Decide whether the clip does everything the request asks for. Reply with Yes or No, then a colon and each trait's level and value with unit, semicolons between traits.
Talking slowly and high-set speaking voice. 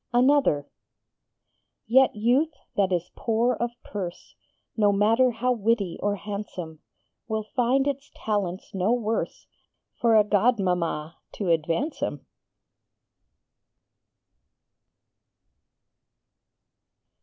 Yes: slow, 95 wpm; high, 215 Hz